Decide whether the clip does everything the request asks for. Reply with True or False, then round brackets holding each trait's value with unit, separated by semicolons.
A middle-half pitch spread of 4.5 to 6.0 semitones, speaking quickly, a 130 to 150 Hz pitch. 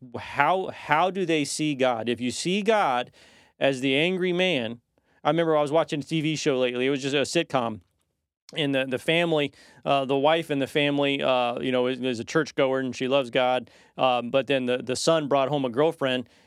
False (3.6 semitones; 215 wpm; 135 Hz)